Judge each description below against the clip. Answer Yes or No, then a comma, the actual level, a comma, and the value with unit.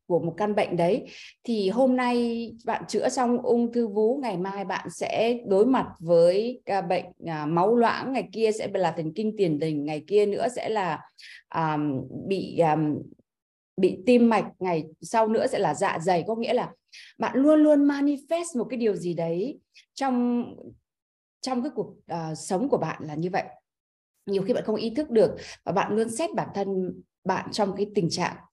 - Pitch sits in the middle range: No, high, 210 Hz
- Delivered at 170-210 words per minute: Yes, average, 190 wpm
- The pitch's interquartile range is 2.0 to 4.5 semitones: No, average, 5.2 semitones